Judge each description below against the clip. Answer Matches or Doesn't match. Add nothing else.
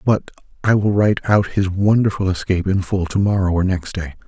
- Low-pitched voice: Matches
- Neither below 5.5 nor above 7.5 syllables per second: Matches